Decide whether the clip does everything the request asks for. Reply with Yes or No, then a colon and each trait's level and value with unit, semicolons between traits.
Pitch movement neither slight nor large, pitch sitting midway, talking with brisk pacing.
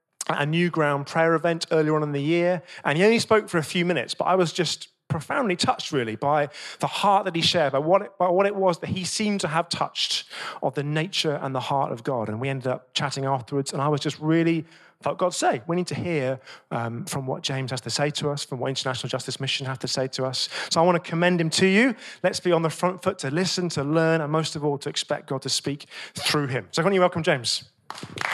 Yes: average, 4.3 semitones; medium, 155 Hz; fast, 265 wpm